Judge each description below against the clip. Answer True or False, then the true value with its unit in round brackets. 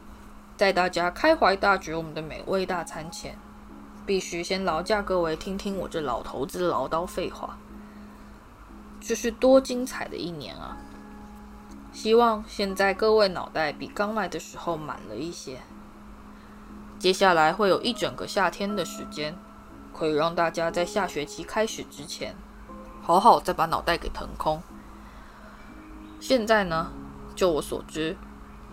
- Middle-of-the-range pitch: True (180 Hz)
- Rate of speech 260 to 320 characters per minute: False (215 characters per minute)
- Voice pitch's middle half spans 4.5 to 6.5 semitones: True (5.1 semitones)